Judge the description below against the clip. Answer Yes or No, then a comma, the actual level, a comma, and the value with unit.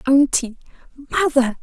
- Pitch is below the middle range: No, very high, 275 Hz